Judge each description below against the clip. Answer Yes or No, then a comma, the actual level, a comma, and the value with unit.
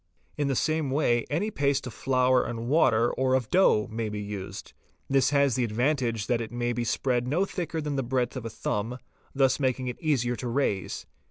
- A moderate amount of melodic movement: Yes, average, 3.1 semitones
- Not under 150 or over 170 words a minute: No, fast, 205 wpm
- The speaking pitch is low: Yes, low, 125 Hz